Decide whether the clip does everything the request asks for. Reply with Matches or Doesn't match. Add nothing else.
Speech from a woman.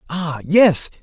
Doesn't match